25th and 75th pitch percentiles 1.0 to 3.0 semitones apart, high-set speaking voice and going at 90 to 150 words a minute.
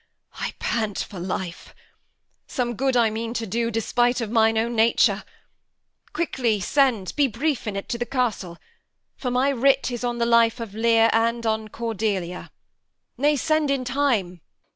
No: narrow, 2.4 semitones; high, 230 Hz; average, 165 wpm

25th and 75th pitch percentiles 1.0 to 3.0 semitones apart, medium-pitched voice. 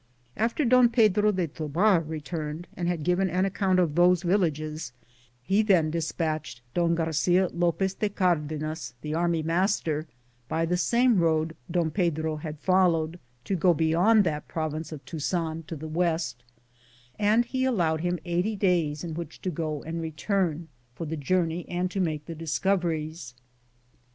Yes: average, 2.7 semitones; medium, 170 Hz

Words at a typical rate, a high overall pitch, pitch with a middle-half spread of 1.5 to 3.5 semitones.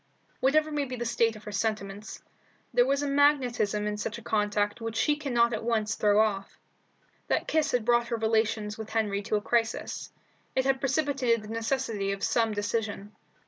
Yes: average, 185 wpm; high, 225 Hz; average, 3.1 semitones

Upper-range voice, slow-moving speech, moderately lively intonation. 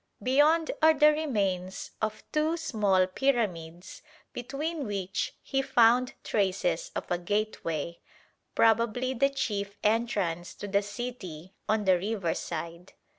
No: high, 215 Hz; slow, 120 wpm; wide, 6.0 semitones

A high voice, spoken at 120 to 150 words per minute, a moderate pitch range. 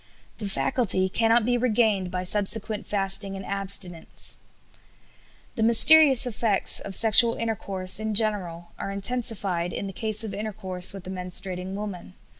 Yes: high, 200 Hz; average, 140 wpm; average, 3.0 semitones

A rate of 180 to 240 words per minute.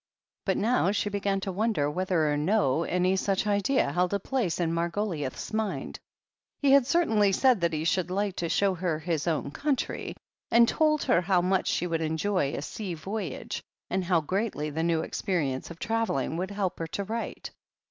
Yes: average, 190 wpm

